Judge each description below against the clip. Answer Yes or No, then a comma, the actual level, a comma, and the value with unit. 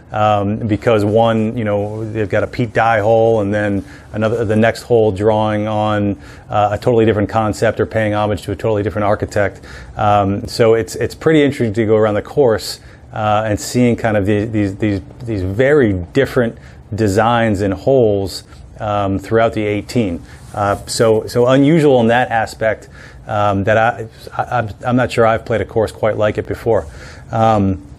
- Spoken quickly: No, average, 185 wpm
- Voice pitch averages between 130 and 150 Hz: No, low, 110 Hz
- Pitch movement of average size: No, narrow, 1.8 semitones